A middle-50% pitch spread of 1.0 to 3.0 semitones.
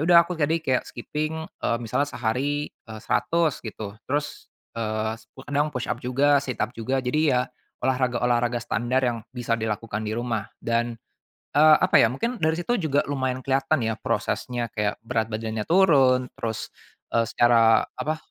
No: average, 4.1 semitones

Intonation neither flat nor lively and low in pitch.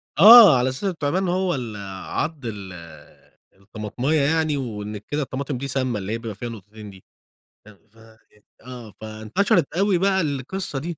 No: wide, 6.9 semitones; low, 130 Hz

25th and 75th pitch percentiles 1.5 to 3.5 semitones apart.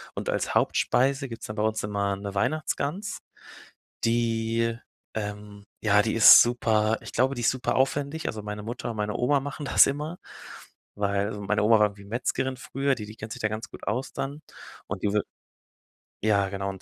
No: average, 4.0 semitones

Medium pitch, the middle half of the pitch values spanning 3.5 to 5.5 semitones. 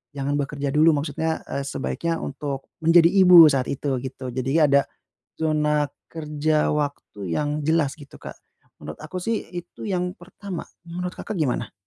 No: medium, 150 Hz; average, 3.1 semitones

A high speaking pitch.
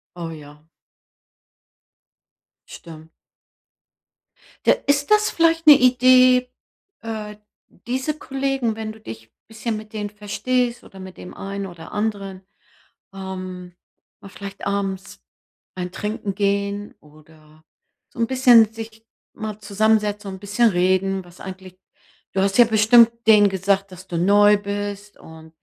Yes: high, 205 Hz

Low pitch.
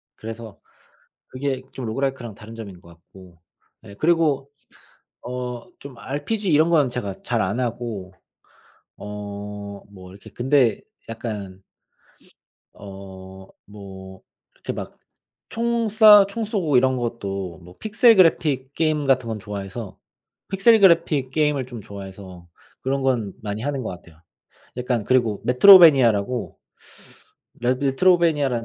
Yes: low, 120 Hz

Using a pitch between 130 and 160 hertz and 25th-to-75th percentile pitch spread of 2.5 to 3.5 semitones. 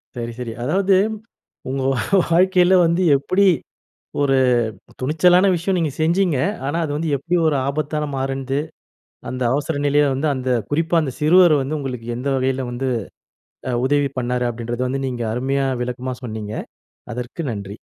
No: medium, 140 Hz; average, 4.1 semitones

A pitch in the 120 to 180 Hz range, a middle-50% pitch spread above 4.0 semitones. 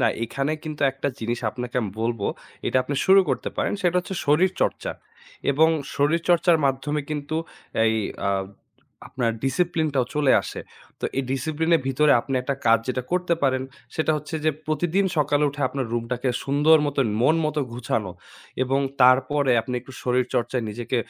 No: medium, 140 Hz; average, 3.6 semitones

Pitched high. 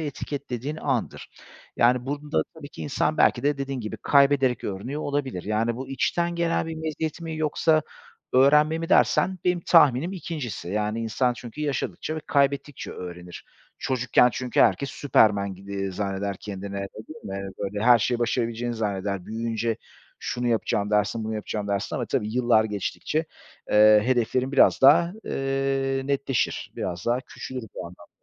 No: low, 125 Hz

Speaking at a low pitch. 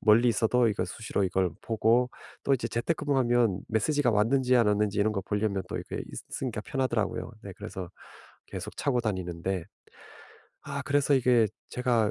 Yes: low, 115 Hz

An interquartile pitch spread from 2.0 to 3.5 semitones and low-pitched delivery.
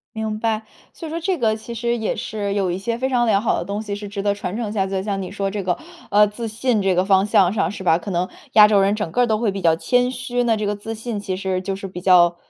No: narrow, 2.6 semitones; high, 205 Hz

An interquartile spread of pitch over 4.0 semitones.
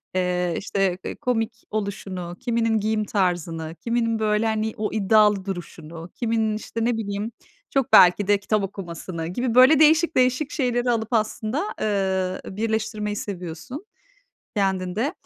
No: average, 3.5 semitones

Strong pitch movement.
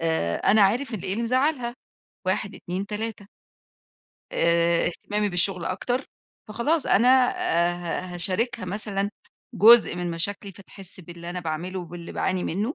No: average, 4.3 semitones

